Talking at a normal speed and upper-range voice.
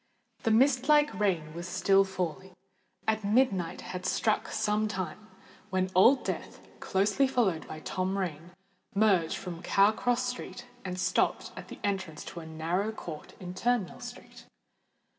Yes: average, 150 wpm; high, 195 Hz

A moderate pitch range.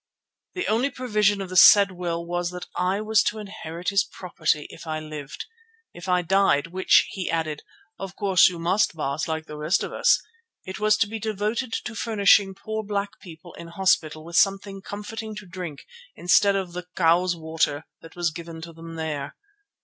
Yes: average, 3.6 semitones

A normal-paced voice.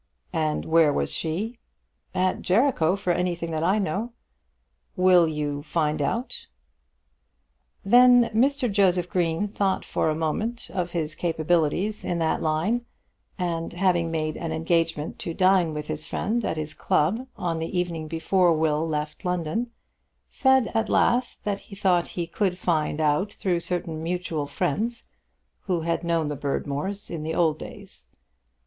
Yes: average, 150 wpm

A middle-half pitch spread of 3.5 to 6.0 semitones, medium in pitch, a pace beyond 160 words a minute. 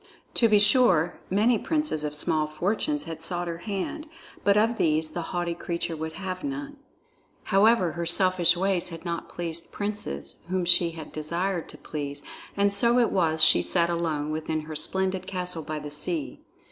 Yes: average, 3.9 semitones; medium, 175 Hz; average, 175 wpm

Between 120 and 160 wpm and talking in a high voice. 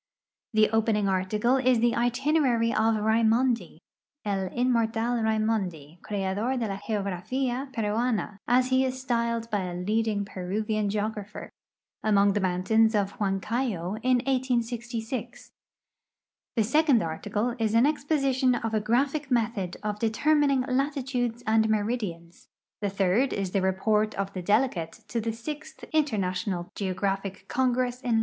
Yes: average, 140 wpm; high, 225 Hz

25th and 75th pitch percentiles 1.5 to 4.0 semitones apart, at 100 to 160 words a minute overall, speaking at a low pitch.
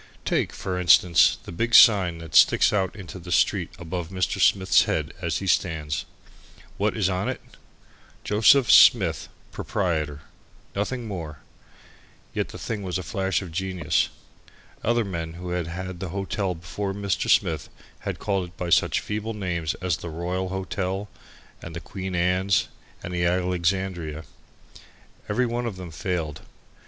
Yes: narrow, 2.5 semitones; average, 155 wpm; very low, 90 Hz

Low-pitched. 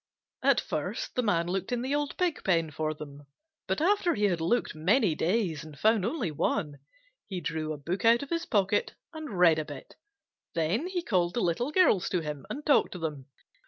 No: medium, 185 Hz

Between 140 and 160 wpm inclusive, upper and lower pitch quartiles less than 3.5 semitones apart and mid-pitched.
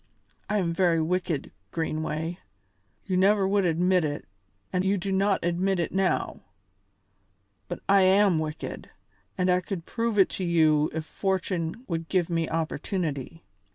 Yes: average, 150 wpm; average, 2.8 semitones; medium, 180 Hz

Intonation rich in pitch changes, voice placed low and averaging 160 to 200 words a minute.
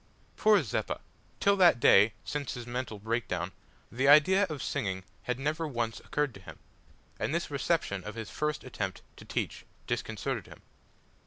Yes: wide, 6.0 semitones; low, 125 Hz; average, 165 wpm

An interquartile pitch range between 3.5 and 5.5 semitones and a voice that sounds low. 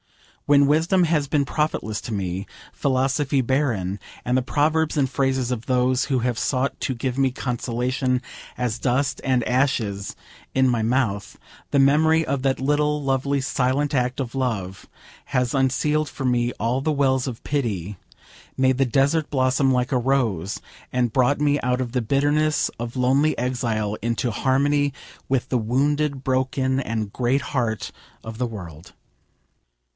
No: narrow, 2.6 semitones; low, 130 Hz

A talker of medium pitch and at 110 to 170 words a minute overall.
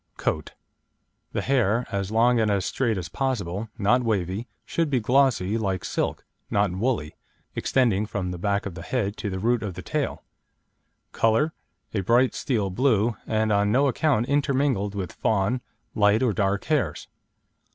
No: low, 110 Hz; average, 160 wpm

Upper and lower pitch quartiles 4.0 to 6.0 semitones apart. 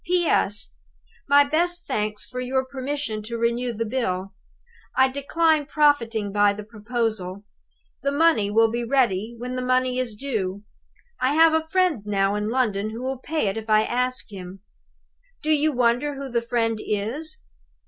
Yes: average, 4.8 semitones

